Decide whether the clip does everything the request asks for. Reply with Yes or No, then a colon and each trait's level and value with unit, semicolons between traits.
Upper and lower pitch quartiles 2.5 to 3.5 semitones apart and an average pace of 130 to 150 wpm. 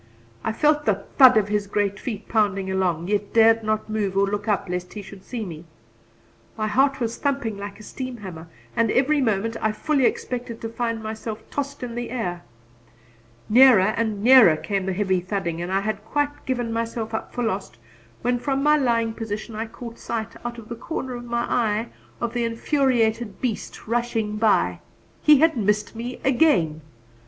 No: average, 3.0 semitones; average, 185 wpm